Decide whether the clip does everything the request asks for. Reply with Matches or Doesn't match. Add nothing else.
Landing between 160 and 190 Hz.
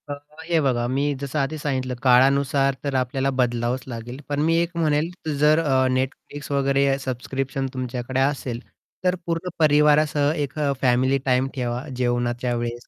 Doesn't match